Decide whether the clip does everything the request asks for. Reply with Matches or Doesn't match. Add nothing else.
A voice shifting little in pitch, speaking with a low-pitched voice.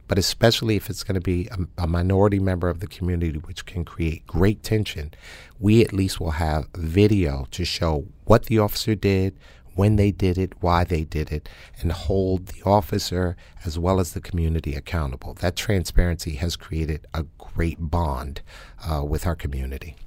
Doesn't match